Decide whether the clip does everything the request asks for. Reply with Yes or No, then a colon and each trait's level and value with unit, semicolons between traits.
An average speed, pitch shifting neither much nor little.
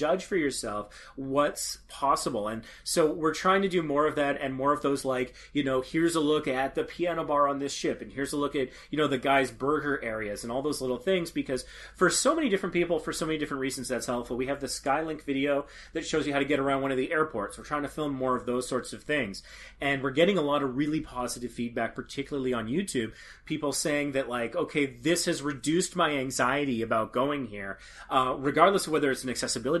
No: fast, 240 wpm; average, 3.1 semitones